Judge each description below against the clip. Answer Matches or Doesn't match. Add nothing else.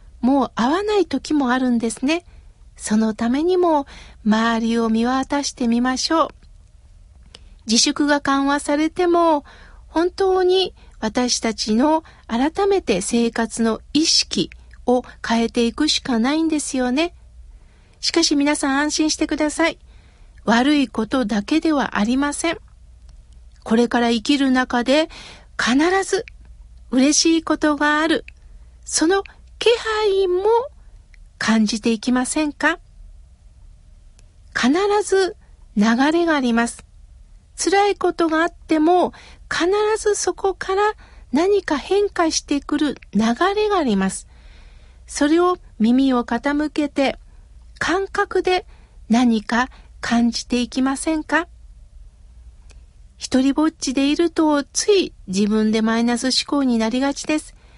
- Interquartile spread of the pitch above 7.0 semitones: Doesn't match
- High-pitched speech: Matches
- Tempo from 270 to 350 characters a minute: Doesn't match